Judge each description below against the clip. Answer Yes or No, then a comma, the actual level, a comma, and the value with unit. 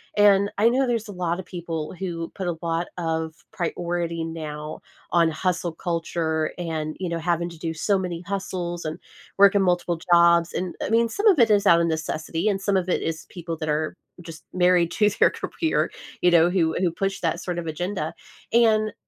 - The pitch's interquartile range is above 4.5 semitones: No, average, 2.8 semitones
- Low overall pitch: No, medium, 175 Hz